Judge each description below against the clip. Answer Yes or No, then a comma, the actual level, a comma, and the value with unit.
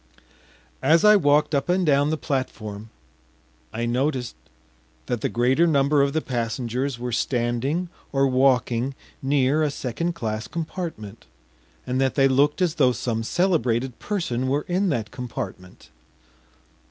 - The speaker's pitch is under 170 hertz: Yes, low, 135 Hz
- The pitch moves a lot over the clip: No, average, 4.2 semitones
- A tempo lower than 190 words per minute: Yes, average, 140 wpm